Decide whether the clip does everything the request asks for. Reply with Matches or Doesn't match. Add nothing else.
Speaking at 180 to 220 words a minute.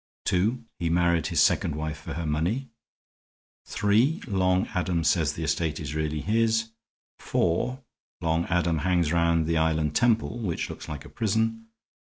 Doesn't match